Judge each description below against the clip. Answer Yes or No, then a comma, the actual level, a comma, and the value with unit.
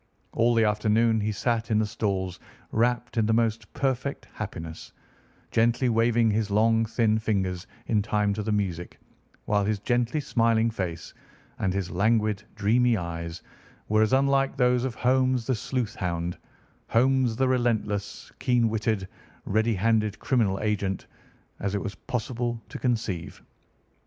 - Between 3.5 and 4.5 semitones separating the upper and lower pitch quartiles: No, average, 2.8 semitones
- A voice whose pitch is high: No, low, 110 Hz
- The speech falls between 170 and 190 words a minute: No, average, 145 wpm